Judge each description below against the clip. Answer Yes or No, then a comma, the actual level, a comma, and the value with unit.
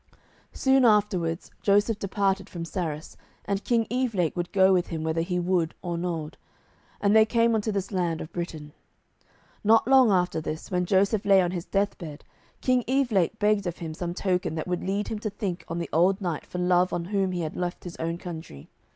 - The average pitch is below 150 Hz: No, medium, 185 Hz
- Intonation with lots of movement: No, average, 3.3 semitones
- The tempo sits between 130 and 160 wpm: No, fast, 205 wpm